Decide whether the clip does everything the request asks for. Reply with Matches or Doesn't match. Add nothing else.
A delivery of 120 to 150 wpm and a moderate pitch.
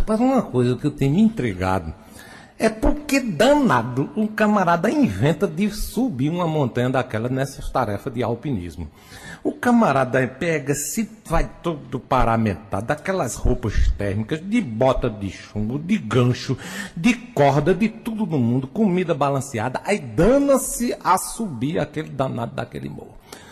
Matches